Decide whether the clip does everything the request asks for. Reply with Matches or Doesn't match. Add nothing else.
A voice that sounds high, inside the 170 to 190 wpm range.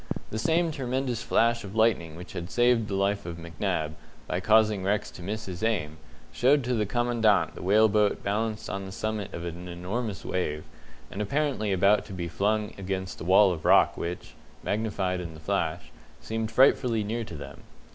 Doesn't match